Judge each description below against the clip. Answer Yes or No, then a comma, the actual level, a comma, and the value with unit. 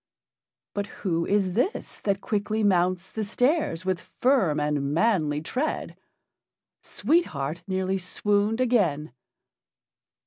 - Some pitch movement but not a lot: Yes, average, 4.8 semitones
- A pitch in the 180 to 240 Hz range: Yes, high, 190 Hz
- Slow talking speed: Yes, slow, 110 wpm